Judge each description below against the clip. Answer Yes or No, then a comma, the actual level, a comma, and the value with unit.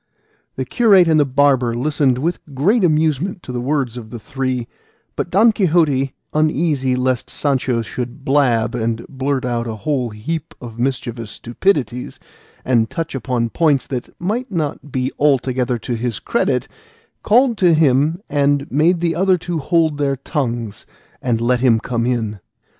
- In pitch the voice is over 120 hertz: Yes, low, 135 Hz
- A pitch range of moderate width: Yes, average, 4.4 semitones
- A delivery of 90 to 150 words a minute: No, average, 160 wpm